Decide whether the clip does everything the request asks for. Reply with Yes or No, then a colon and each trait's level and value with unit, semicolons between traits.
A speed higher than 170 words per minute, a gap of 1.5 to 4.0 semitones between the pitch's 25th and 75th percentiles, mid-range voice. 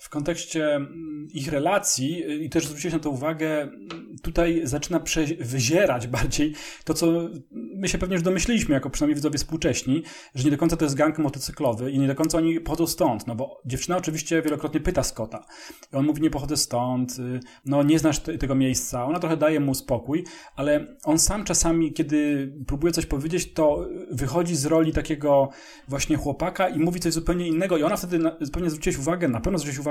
Yes: average, 195 wpm; average, 2.7 semitones; medium, 155 Hz